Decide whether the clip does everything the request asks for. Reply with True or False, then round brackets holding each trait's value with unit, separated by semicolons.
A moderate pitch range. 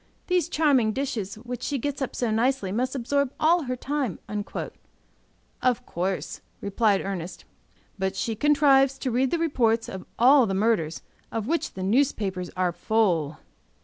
False (5.7 semitones)